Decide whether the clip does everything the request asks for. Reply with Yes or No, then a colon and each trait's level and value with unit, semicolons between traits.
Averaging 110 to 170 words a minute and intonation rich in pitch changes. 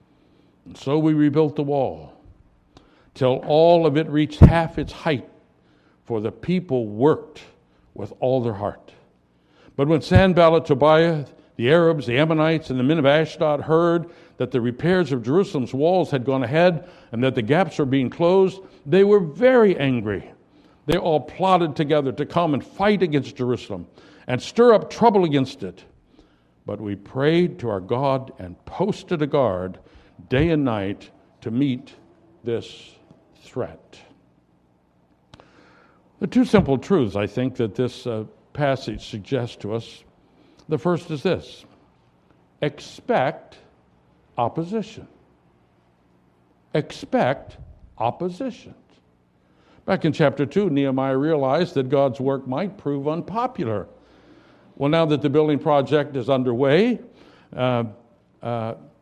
Yes: slow, 135 wpm; wide, 6.1 semitones